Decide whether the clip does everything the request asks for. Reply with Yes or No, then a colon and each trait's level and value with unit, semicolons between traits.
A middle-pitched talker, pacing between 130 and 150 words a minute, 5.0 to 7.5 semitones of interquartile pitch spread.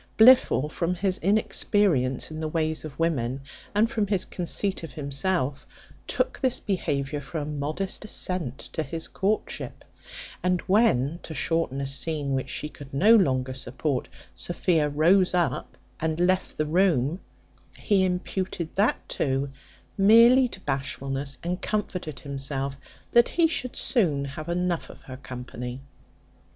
Yes: medium, 160 Hz; average, 140 wpm; wide, 5.4 semitones